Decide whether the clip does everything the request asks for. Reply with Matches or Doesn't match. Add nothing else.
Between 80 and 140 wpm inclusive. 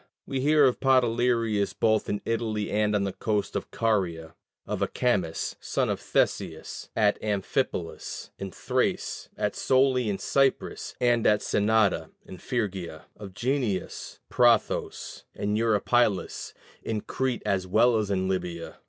Matches